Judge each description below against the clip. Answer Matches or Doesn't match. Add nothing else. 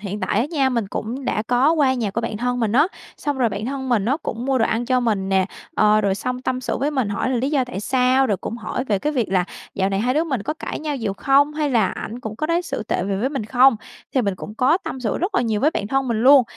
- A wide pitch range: Doesn't match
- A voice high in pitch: Matches